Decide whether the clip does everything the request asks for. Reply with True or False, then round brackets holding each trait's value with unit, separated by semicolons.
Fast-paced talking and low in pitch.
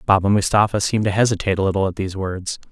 True (220 wpm; 100 Hz)